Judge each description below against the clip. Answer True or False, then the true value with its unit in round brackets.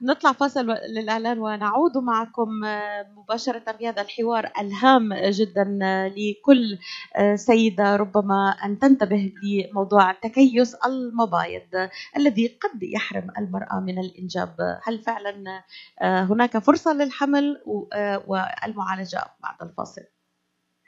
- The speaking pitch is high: True (210 Hz)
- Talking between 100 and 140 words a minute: False (90 wpm)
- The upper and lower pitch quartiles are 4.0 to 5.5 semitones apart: False (3.4 semitones)